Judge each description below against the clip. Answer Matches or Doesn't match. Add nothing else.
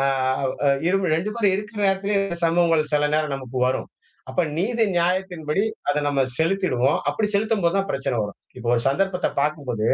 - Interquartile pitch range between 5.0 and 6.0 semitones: Matches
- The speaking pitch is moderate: Matches